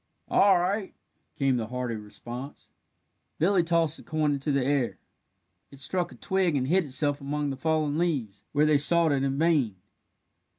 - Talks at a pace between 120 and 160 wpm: No, average, 170 wpm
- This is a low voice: No, medium, 145 Hz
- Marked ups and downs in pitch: No, average, 3.8 semitones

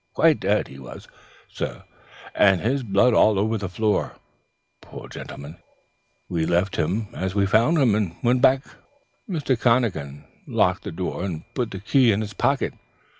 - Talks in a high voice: No, low, 105 Hz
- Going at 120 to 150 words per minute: No, average, 165 wpm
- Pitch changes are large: No, average, 4.6 semitones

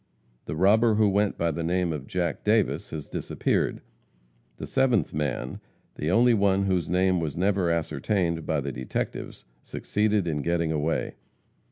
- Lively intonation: No, average, 4.3 semitones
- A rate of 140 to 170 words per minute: Yes, average, 155 wpm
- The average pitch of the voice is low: Yes, very low, 85 Hz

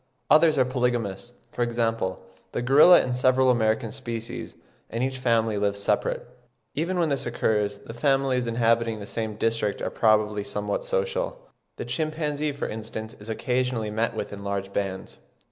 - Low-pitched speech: Yes, low, 115 Hz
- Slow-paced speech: No, average, 160 wpm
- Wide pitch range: No, average, 3.7 semitones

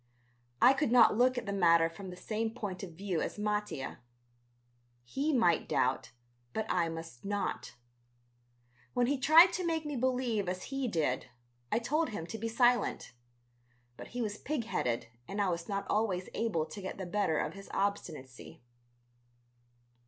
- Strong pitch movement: Yes, wide, 5.7 semitones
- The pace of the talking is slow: No, average, 165 wpm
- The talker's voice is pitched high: Yes, high, 210 Hz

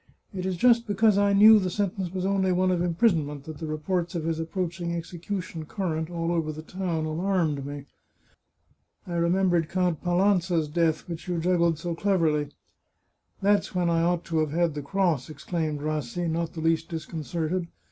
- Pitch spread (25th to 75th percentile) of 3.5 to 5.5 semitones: No, narrow, 2.6 semitones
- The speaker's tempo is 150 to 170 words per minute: No, average, 180 wpm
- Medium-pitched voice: Yes, medium, 170 Hz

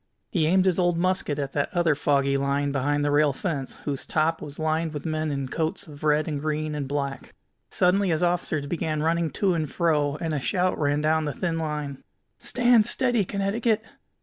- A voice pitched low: No, medium, 155 Hz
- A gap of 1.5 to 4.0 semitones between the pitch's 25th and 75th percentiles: Yes, average, 3.4 semitones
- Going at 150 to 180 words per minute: No, average, 200 wpm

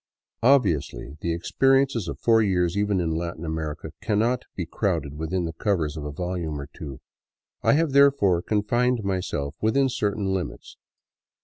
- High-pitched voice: No, very low, 95 Hz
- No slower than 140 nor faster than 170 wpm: Yes, average, 150 wpm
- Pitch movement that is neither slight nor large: No, wide, 5.7 semitones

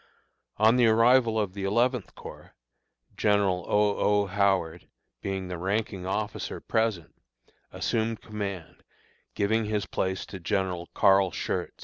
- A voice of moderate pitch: No, low, 100 Hz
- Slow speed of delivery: Yes, slow, 125 wpm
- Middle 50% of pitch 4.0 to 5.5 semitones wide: No, average, 2.7 semitones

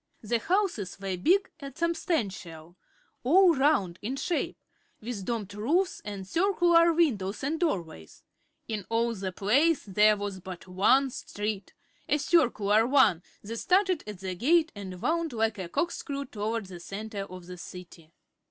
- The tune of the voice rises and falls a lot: Yes, wide, 8.5 semitones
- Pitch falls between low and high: No, high, 220 Hz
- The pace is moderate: Yes, average, 150 wpm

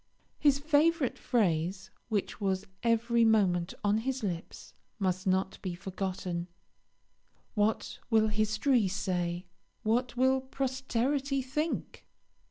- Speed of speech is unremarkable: No, slow, 105 wpm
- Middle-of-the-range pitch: No, high, 220 Hz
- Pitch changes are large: Yes, wide, 5.7 semitones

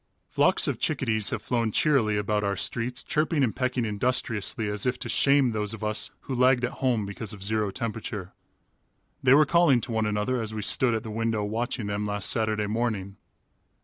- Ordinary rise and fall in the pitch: Yes, average, 3.2 semitones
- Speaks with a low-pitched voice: Yes, low, 110 Hz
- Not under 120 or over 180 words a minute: No, average, 195 wpm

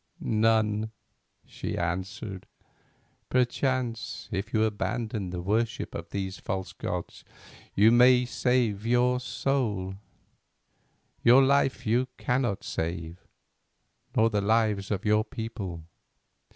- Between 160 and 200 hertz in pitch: No, low, 110 Hz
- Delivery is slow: Yes, slow, 105 wpm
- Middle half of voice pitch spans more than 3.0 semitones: Yes, average, 3.9 semitones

